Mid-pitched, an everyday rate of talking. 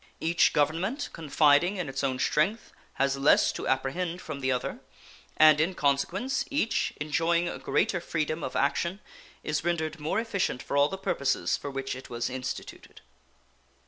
Yes: medium, 155 Hz; average, 160 wpm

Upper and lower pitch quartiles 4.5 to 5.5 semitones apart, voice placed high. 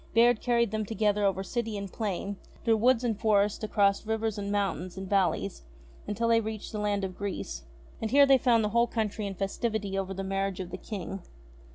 No: narrow, 2.4 semitones; high, 210 Hz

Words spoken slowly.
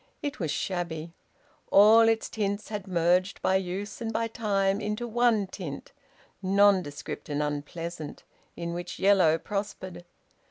Yes: slow, 130 wpm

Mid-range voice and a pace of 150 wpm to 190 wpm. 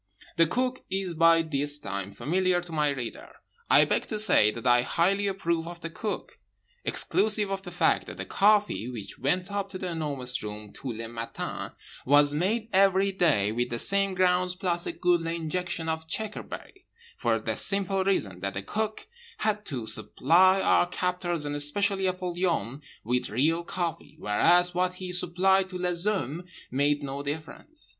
Yes: medium, 175 Hz; average, 170 wpm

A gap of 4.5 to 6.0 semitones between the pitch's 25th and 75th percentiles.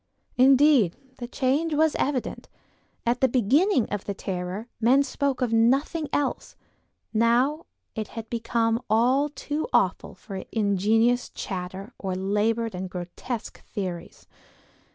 Yes: average, 4.8 semitones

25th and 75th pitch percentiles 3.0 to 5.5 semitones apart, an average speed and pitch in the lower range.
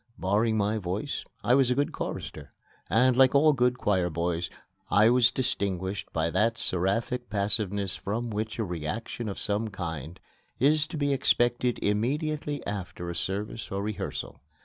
Yes: average, 4.4 semitones; average, 155 wpm; low, 105 Hz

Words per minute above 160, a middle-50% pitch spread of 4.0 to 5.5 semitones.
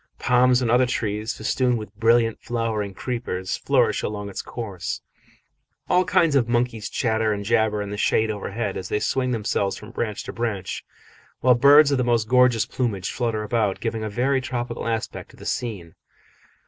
No: average, 175 wpm; average, 2.7 semitones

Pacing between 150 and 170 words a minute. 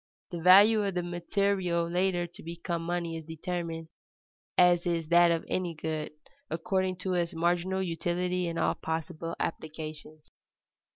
No: average, 140 wpm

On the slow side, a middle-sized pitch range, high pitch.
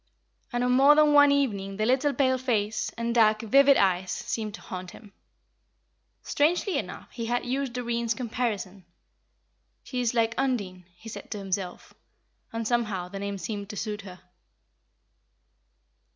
No: average, 150 wpm; average, 4.1 semitones; high, 225 Hz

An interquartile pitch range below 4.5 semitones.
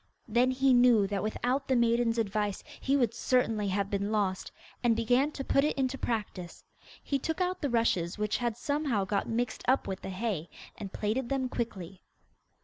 Yes: average, 4.1 semitones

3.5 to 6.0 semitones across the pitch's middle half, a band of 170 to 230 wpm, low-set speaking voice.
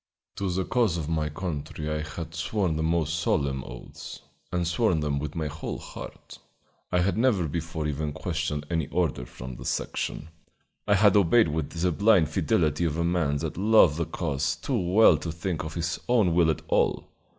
No: average, 3.0 semitones; average, 190 wpm; very low, 80 Hz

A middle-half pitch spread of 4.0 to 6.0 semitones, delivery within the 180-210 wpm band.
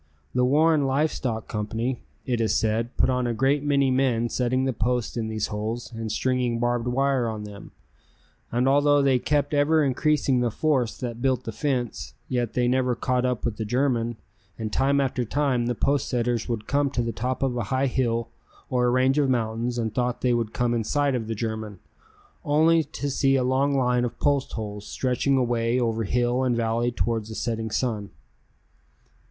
No: narrow, 2.6 semitones; average, 195 wpm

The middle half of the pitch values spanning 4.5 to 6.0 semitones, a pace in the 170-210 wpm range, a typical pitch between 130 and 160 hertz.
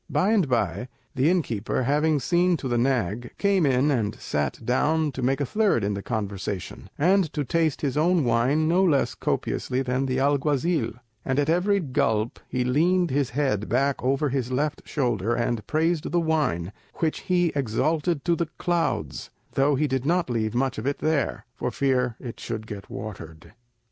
Yes: average, 5.0 semitones; average, 180 wpm; low, 135 Hz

